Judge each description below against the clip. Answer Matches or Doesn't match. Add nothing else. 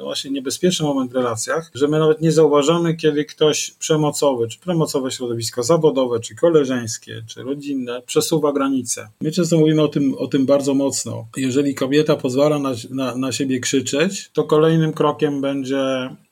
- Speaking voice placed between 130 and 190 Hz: Matches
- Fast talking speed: Matches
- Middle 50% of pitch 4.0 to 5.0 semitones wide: Doesn't match